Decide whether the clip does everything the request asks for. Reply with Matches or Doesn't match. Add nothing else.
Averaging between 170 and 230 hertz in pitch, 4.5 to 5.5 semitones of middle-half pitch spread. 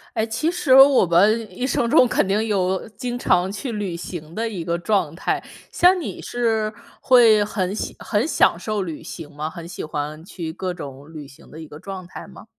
Matches